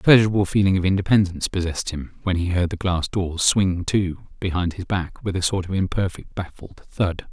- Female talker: No, male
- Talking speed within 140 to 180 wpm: No, fast, 205 wpm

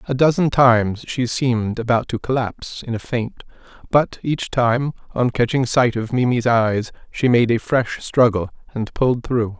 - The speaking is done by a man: Yes, male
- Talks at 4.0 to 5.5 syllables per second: Yes, 4.6 syllables/s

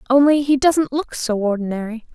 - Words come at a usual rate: Yes, average, 170 wpm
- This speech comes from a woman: Yes, female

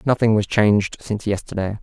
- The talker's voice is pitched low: Yes, low, 105 Hz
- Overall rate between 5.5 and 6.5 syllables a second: Yes, 5.9 syllables/s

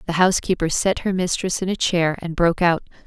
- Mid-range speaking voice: Yes, medium, 175 Hz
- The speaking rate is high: Yes, fast, 215 wpm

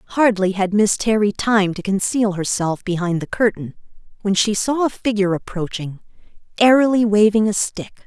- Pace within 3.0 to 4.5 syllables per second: No, 5.1 syllables/s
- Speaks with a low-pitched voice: No, high, 205 Hz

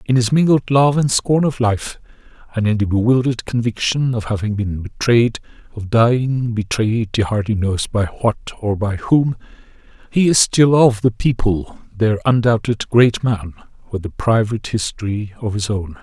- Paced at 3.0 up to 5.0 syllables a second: Yes, 4.7 syllables/s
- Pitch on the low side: Yes, low, 115 Hz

